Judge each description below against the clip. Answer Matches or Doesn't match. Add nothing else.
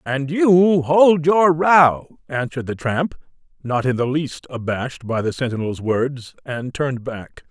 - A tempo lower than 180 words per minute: Matches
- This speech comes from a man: Matches